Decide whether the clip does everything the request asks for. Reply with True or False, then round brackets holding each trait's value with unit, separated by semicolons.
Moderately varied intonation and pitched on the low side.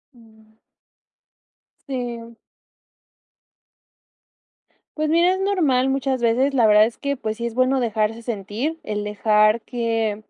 False (3.6 semitones; 235 Hz)